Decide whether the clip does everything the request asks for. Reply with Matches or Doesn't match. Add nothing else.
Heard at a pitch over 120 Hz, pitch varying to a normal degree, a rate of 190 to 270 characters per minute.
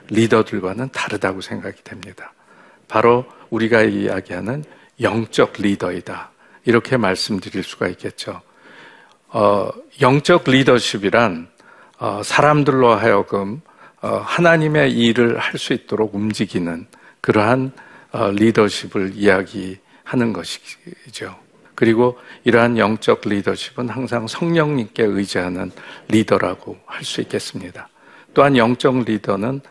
Doesn't match